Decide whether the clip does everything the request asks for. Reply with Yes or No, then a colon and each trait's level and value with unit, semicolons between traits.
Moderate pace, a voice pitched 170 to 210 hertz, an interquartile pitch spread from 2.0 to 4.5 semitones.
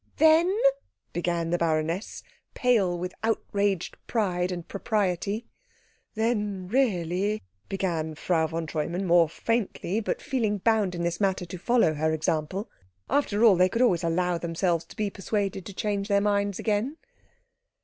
Yes: average, 150 wpm; high, 190 Hz; average, 3.7 semitones